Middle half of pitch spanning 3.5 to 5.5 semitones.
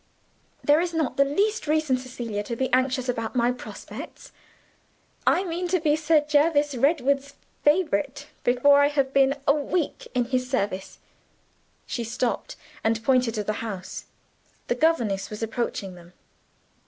Yes: average, 4.0 semitones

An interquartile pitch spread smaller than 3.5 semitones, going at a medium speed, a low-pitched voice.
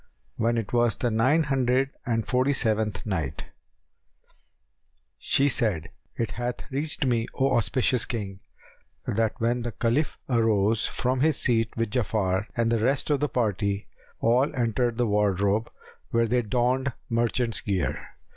Yes: average, 2.9 semitones; average, 145 wpm; low, 115 Hz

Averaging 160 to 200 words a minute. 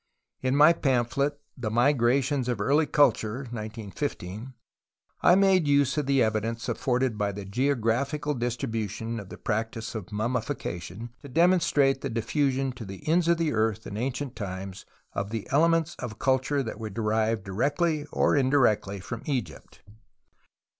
No: average, 145 wpm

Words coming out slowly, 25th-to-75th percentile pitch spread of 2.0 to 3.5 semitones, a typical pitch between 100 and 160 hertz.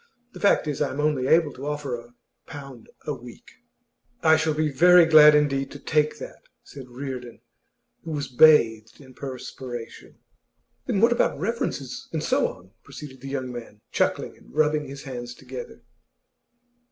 No: average, 165 wpm; average, 3.2 semitones; medium, 140 Hz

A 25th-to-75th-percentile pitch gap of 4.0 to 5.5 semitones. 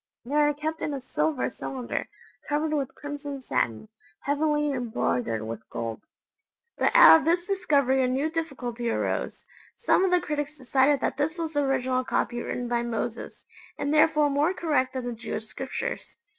No: average, 3.6 semitones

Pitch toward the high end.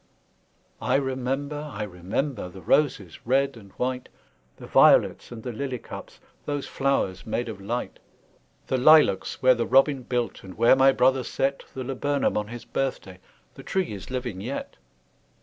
No: low, 125 Hz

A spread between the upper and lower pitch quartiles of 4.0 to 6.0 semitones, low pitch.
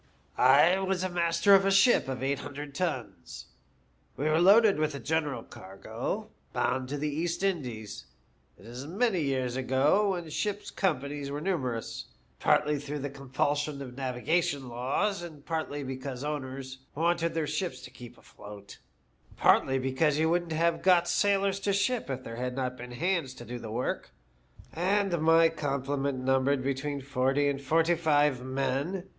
No: average, 4.5 semitones; medium, 145 Hz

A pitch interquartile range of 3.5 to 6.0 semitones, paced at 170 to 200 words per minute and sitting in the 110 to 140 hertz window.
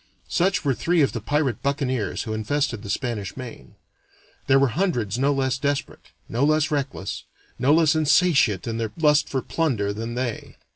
Yes: average, 4.6 semitones; average, 175 wpm; low, 135 Hz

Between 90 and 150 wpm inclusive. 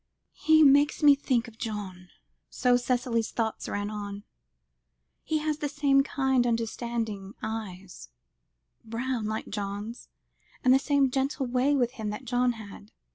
Yes: slow, 135 wpm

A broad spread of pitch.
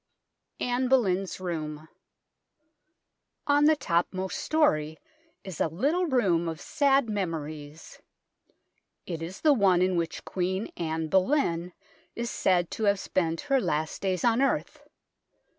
Yes: wide, 6.8 semitones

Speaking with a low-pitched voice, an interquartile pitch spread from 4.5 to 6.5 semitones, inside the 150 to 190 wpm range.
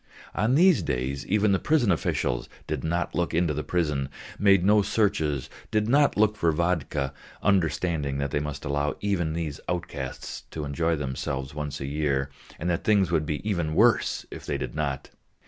Yes: very low, 80 Hz; wide, 5.4 semitones; average, 180 wpm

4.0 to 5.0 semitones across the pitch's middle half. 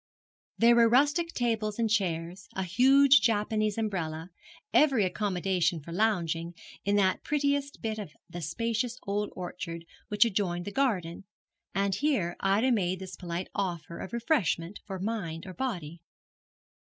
Yes: average, 4.7 semitones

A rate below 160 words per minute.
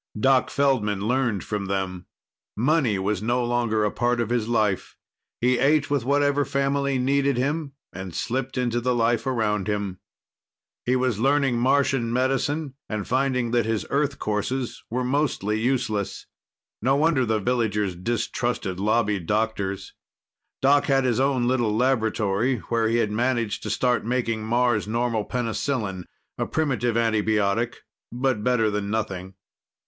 Yes: average, 145 wpm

